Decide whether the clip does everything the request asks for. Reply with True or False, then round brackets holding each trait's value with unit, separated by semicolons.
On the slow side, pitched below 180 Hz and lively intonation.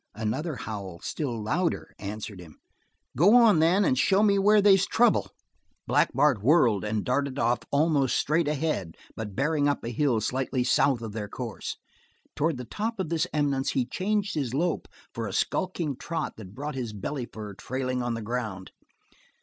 False (175 wpm; 135 Hz; 6.4 semitones)